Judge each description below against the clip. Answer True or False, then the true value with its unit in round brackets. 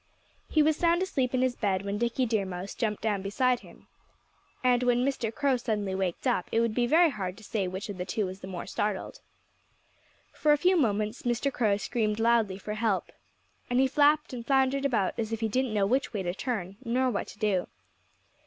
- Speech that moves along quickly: True (215 wpm)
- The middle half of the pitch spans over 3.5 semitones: True (4.3 semitones)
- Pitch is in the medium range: False (230 Hz)